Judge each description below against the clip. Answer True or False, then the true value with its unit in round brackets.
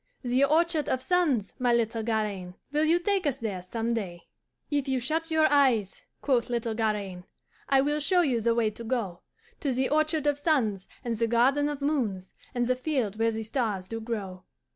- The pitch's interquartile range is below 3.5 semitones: False (4.9 semitones)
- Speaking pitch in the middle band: False (240 Hz)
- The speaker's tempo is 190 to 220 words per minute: True (195 wpm)